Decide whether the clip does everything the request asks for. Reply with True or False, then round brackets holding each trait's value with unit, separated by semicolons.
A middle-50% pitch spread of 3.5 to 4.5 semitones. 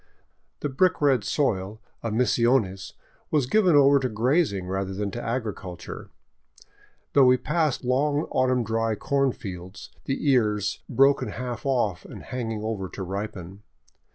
False (4.9 semitones)